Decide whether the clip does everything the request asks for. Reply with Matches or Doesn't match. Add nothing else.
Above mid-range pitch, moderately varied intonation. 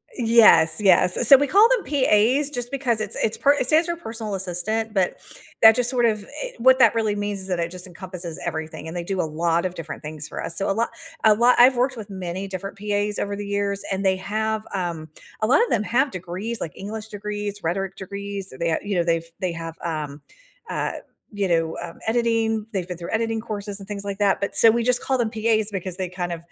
Matches